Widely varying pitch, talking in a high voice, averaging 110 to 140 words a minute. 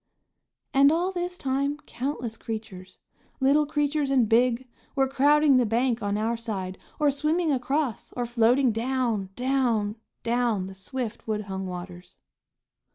No: average, 4.2 semitones; high, 245 Hz; slow, 135 wpm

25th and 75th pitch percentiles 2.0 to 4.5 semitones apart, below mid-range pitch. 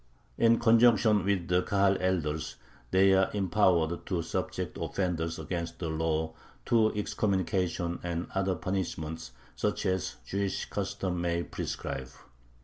Yes: average, 2.7 semitones; very low, 90 Hz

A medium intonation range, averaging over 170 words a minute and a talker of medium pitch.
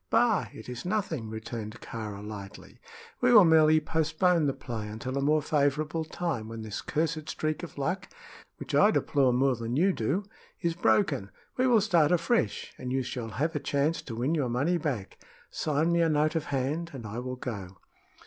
No: wide, 5.8 semitones; average, 190 wpm; medium, 145 Hz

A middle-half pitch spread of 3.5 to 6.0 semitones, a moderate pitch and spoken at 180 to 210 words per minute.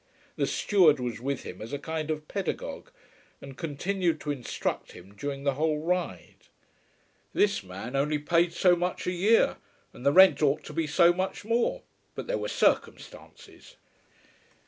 No: average, 4.6 semitones; medium, 155 Hz; average, 165 wpm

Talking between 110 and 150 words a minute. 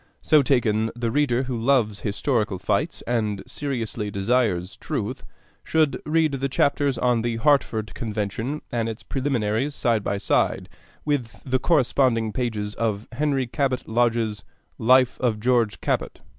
Yes: average, 140 wpm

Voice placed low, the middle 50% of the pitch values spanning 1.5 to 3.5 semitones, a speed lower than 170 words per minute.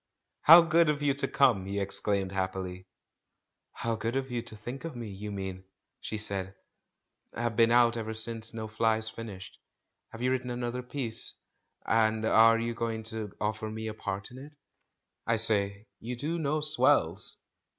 No: low, 115 Hz; average, 2.8 semitones; average, 180 wpm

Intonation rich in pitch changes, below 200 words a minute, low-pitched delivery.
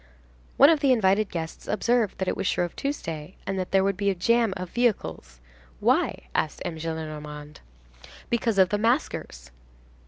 No: wide, 6.5 semitones; average, 155 wpm; medium, 185 Hz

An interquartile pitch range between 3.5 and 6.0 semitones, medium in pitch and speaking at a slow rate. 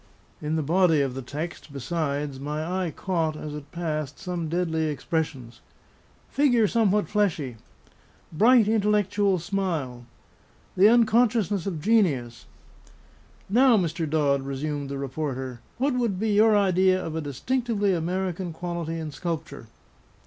Yes: average, 5.3 semitones; medium, 170 Hz; slow, 130 wpm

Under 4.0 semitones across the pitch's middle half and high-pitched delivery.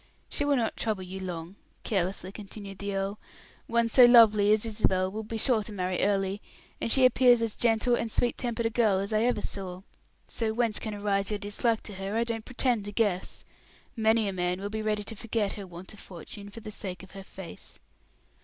Yes: average, 2.8 semitones; high, 210 Hz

